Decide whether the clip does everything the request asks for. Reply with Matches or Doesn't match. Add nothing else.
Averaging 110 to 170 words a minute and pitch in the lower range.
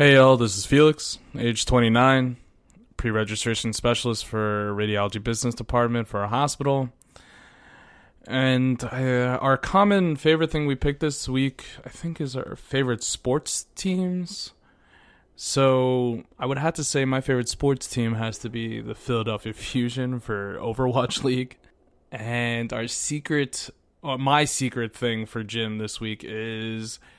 Matches